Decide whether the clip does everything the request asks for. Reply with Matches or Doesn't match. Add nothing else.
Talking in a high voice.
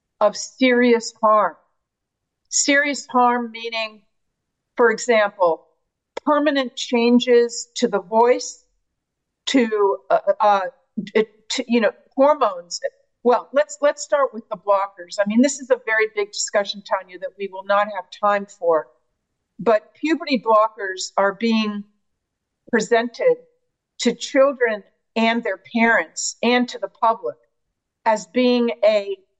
Matches